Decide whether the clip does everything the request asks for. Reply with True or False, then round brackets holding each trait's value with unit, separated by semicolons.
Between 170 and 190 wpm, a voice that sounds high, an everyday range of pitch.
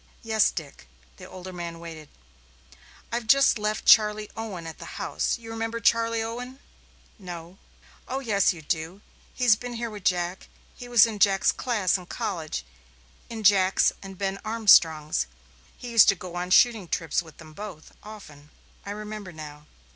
False (160 wpm; 200 Hz; 4.7 semitones)